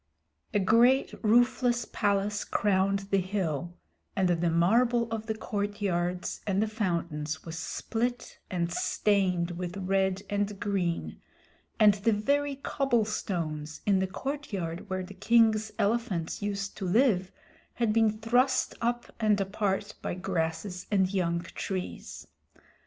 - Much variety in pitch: No, average, 3.5 semitones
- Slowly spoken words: Yes, slow, 130 wpm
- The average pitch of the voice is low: No, high, 200 Hz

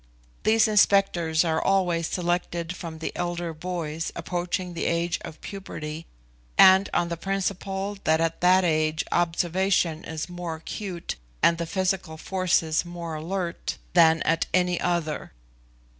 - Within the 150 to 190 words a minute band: No, slow, 135 wpm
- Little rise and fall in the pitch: Yes, narrow, 2.2 semitones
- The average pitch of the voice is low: No, medium, 175 Hz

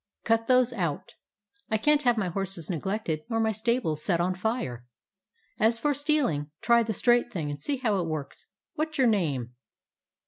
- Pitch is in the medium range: No, high, 220 Hz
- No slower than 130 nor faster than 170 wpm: No, average, 180 wpm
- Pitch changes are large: Yes, wide, 6.4 semitones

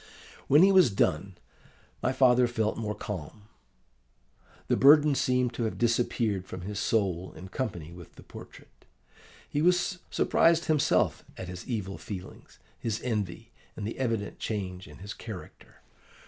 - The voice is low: Yes, low, 110 Hz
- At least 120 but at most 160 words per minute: Yes, average, 145 wpm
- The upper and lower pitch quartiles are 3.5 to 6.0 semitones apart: Yes, average, 5.1 semitones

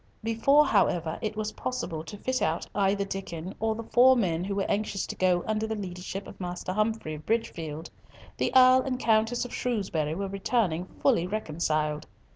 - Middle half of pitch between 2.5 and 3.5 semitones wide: No, average, 4.6 semitones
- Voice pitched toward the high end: Yes, high, 200 Hz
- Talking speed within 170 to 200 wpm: Yes, average, 180 wpm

